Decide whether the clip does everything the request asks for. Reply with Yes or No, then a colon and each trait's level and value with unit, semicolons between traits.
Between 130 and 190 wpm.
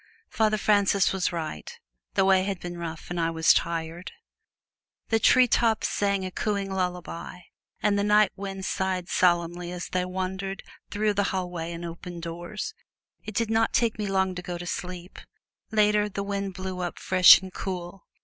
Yes: average, 170 wpm